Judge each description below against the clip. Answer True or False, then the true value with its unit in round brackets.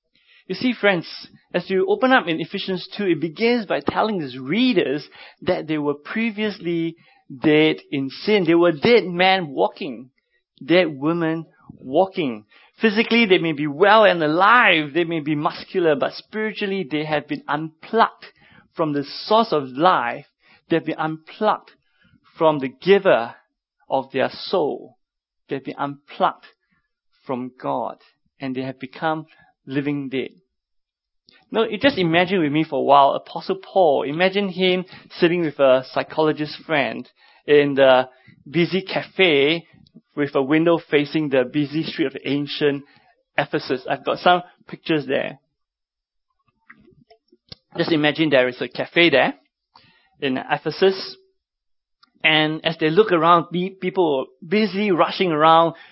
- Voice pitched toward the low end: False (165 Hz)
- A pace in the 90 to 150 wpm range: True (140 wpm)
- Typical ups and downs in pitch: True (4.5 semitones)